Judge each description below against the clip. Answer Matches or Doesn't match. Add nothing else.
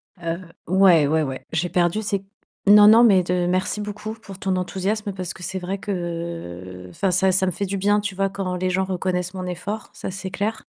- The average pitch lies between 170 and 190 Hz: Matches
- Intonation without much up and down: Matches